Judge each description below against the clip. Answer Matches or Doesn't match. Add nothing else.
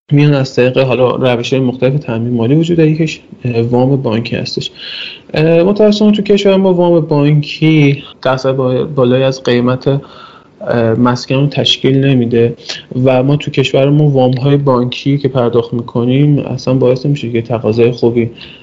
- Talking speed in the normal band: Matches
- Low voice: Matches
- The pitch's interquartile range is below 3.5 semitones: Matches